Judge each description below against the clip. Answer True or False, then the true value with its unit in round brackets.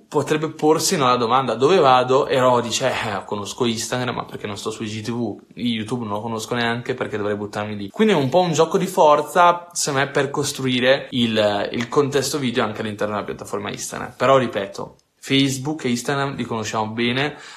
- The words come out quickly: True (190 wpm)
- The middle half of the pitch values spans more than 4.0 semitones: True (4.6 semitones)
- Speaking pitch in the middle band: False (125 Hz)